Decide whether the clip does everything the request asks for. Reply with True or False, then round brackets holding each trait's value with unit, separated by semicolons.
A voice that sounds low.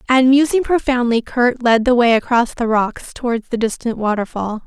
False (240 Hz)